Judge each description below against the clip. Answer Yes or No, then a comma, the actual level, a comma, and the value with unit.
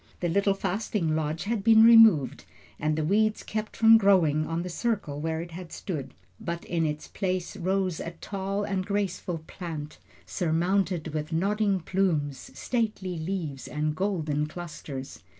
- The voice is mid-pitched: Yes, medium, 175 Hz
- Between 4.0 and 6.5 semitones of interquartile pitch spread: Yes, average, 4.3 semitones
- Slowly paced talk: No, average, 150 wpm